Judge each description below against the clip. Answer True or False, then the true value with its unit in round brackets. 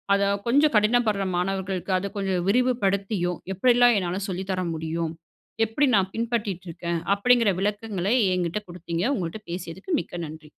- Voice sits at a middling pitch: False (195 Hz)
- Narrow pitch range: False (4.0 semitones)